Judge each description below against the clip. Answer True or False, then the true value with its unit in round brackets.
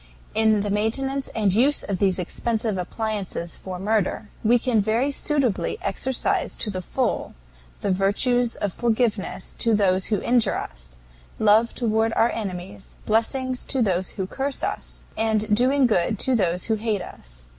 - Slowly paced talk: False (155 wpm)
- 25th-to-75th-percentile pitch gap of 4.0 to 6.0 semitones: False (3.6 semitones)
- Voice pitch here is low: False (220 Hz)